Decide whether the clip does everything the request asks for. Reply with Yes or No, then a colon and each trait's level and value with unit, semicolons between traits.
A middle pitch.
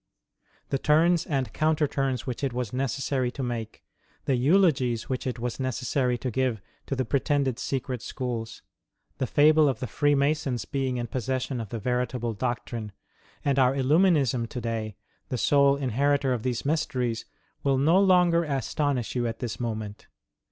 No: low, 130 Hz